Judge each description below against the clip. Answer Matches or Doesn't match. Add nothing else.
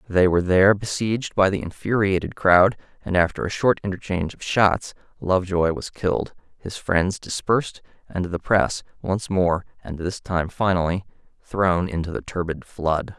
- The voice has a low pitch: Matches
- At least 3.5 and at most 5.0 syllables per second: Matches